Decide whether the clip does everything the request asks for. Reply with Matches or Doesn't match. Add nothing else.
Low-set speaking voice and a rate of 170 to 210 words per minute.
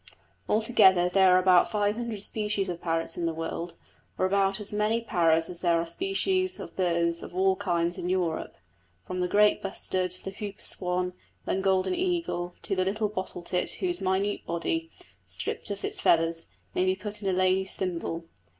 Doesn't match